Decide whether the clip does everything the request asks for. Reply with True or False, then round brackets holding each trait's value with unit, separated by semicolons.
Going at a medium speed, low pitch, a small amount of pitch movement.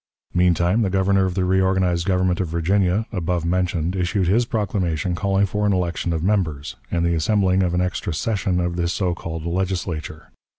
True (180 wpm; 90 Hz; 2.0 semitones)